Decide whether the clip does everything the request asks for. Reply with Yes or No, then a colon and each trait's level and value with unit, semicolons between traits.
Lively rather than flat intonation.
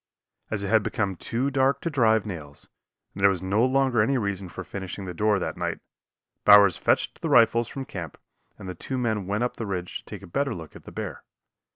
No: average, 4.2 semitones